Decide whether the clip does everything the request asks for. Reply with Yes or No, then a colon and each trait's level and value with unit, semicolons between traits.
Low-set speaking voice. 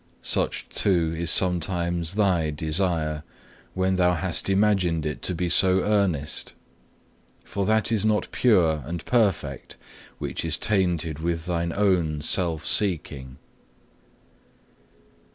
Yes: very low, 85 Hz